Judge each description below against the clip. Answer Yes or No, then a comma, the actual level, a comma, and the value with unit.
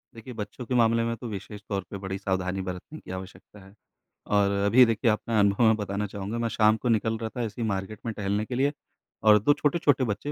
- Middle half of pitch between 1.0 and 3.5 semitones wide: Yes, average, 2.7 semitones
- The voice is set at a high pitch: No, low, 110 Hz